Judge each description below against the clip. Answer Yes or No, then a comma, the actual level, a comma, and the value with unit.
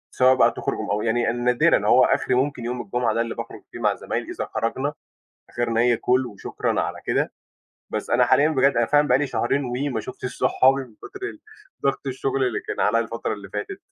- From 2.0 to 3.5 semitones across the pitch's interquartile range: Yes, narrow, 2.5 semitones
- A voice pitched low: Yes, low, 125 Hz